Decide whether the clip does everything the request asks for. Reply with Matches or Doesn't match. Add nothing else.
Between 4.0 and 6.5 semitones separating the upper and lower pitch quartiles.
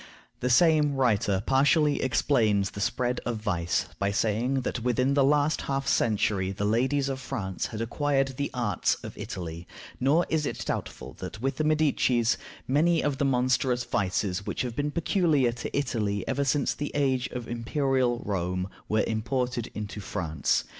Matches